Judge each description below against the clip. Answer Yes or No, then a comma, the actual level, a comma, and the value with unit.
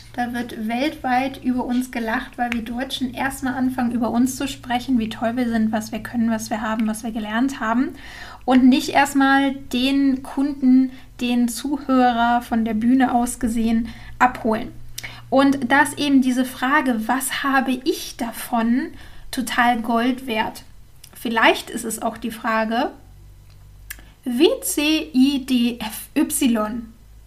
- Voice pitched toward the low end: No, high, 245 Hz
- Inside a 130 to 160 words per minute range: Yes, average, 135 wpm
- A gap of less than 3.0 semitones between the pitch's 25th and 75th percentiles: Yes, narrow, 2.6 semitones